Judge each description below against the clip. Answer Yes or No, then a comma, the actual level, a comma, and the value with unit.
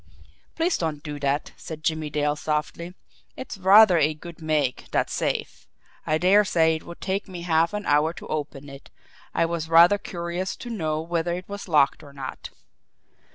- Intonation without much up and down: No, average, 3.0 semitones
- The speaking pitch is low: No, medium, 165 Hz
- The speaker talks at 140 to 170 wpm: No, average, 180 wpm